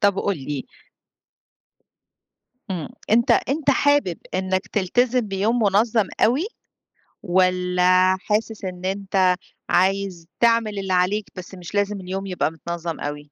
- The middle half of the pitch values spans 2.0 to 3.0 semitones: Yes, narrow, 2.6 semitones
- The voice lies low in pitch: No, high, 190 Hz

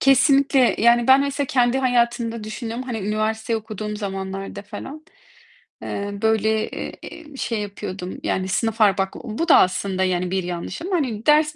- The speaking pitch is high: Yes, high, 220 Hz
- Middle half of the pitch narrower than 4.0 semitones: No, average, 4.4 semitones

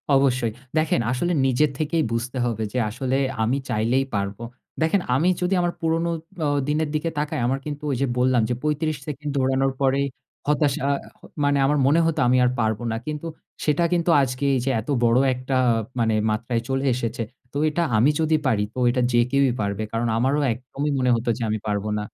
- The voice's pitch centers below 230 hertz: Yes, low, 135 Hz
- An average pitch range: Yes, average, 3.9 semitones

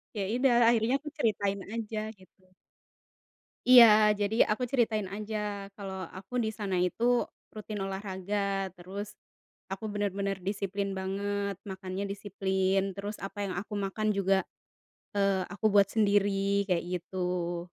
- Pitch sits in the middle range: No, high, 200 Hz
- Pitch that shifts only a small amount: Yes, narrow, 1.8 semitones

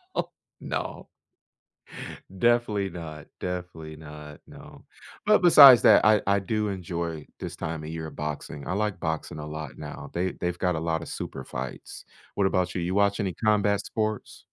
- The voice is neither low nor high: No, very low, 90 Hz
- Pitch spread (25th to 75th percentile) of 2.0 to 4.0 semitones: No, average, 4.5 semitones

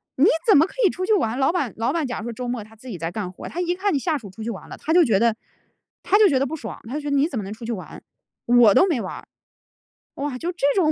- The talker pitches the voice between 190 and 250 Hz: No, very high, 260 Hz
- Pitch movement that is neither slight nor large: No, wide, 6.7 semitones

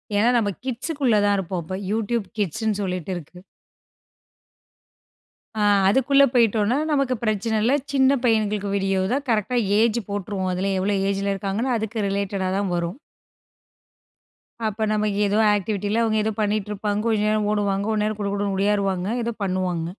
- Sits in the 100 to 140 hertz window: No, high, 205 Hz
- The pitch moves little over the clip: Yes, narrow, 2.3 semitones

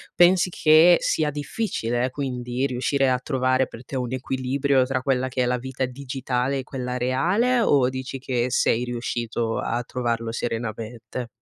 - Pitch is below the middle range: Yes, low, 130 Hz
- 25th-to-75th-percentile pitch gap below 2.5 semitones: Yes, narrow, 2.0 semitones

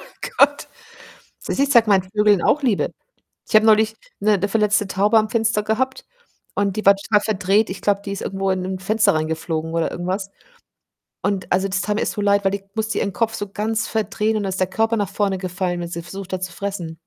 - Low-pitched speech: No, high, 200 Hz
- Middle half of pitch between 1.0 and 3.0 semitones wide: Yes, narrow, 2.5 semitones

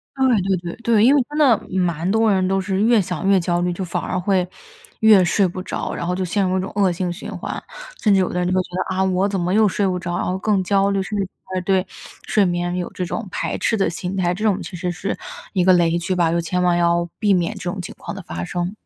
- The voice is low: No, medium, 185 Hz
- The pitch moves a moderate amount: No, narrow, 2.1 semitones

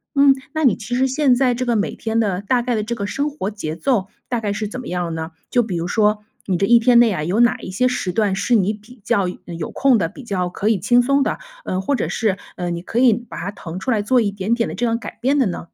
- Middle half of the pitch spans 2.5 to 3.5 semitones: No, average, 4.3 semitones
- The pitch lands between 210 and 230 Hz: Yes, high, 220 Hz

